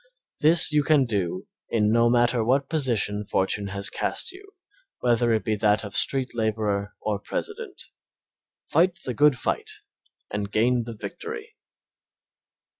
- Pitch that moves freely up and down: Yes, wide, 6.1 semitones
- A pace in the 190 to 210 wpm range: No, average, 140 wpm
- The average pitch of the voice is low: Yes, low, 120 Hz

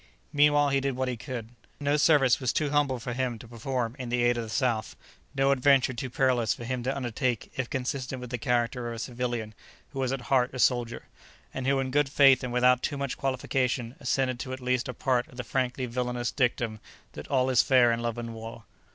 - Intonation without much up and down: Yes, narrow, 1.9 semitones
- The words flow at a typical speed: No, fast, 230 wpm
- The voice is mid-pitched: No, low, 125 Hz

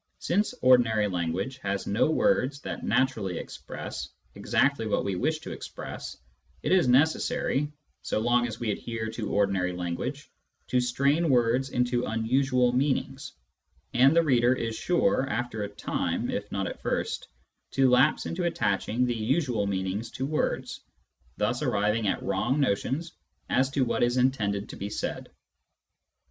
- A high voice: No, low, 125 Hz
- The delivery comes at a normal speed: Yes, average, 150 wpm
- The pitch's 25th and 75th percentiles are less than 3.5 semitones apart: No, average, 4.1 semitones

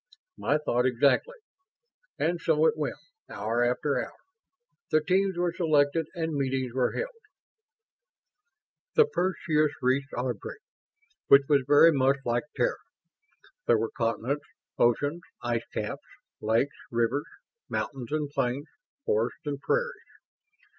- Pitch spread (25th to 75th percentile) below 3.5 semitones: No, average, 4.4 semitones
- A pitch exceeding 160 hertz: No, medium, 145 Hz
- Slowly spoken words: Yes, slow, 120 wpm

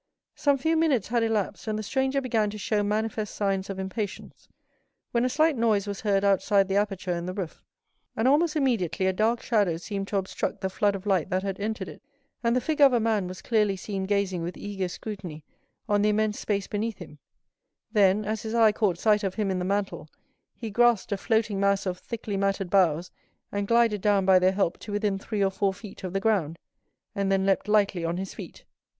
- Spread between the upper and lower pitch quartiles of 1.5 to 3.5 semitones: Yes, narrow, 2.4 semitones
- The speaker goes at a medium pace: No, fast, 215 wpm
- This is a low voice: No, high, 205 Hz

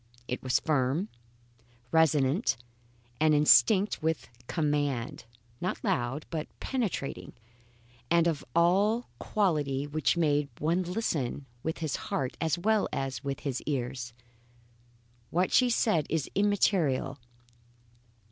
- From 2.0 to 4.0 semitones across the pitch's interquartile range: No, average, 4.4 semitones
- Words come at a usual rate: No, slow, 110 wpm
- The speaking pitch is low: No, medium, 155 Hz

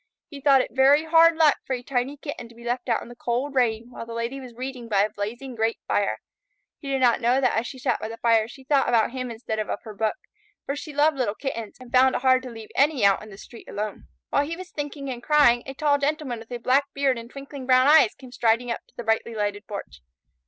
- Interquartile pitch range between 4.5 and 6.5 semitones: No, average, 3.2 semitones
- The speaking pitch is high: Yes, very high, 250 Hz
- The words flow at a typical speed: No, fast, 260 wpm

